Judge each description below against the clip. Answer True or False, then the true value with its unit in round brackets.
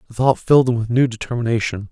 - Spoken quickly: True (220 wpm)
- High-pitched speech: False (120 Hz)